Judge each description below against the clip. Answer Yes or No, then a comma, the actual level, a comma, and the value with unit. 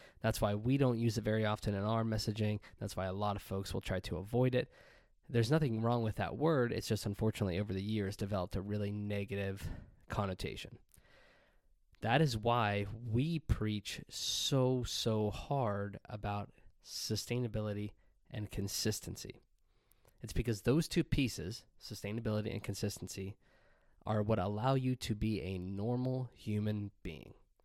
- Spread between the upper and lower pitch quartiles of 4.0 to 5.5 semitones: No, average, 2.8 semitones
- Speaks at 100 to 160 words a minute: Yes, average, 150 wpm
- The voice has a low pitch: Yes, low, 105 Hz